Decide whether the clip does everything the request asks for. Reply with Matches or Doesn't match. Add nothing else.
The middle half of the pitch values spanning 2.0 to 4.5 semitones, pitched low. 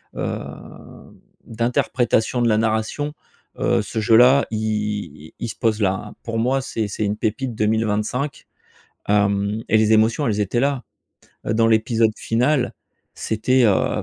Matches